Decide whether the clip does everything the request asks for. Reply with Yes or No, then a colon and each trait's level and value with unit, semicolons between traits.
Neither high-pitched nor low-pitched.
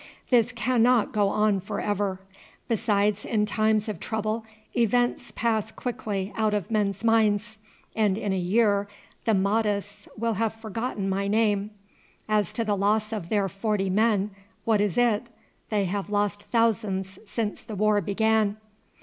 No: high, 210 Hz